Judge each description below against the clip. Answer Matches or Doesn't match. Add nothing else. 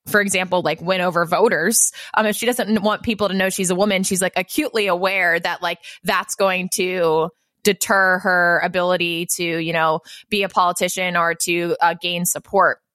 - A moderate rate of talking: Matches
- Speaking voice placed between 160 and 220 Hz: Matches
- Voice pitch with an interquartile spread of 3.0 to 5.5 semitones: Doesn't match